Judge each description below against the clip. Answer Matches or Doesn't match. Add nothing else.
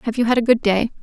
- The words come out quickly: Matches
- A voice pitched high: Matches